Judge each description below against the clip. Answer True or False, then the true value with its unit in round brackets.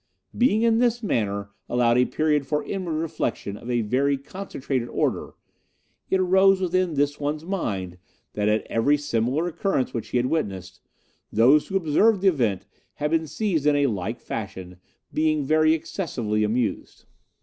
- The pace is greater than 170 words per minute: False (160 wpm)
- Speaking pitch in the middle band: True (145 Hz)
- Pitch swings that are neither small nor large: False (6.8 semitones)